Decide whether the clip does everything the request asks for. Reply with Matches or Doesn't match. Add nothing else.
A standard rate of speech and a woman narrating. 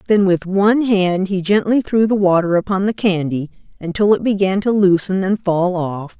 Matches